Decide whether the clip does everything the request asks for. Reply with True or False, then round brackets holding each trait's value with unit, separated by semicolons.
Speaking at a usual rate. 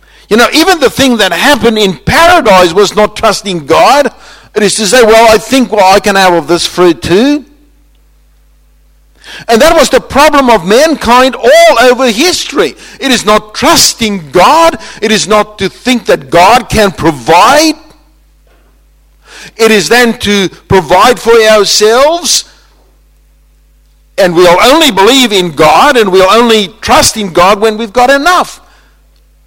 True (155 wpm)